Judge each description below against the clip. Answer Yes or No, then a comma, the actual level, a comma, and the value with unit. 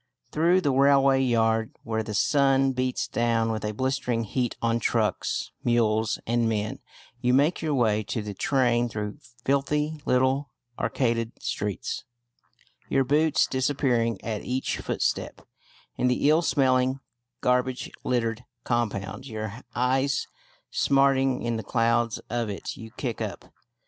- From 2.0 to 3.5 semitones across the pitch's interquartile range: Yes, average, 3.0 semitones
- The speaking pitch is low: Yes, low, 125 Hz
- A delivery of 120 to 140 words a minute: Yes, slow, 135 wpm